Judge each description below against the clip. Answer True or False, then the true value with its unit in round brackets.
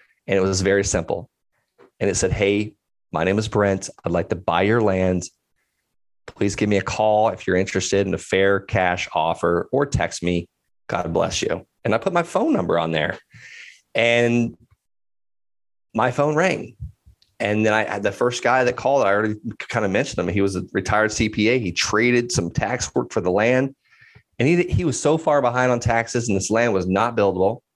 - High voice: False (105 Hz)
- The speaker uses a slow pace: False (200 wpm)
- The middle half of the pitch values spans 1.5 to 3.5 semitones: False (3.9 semitones)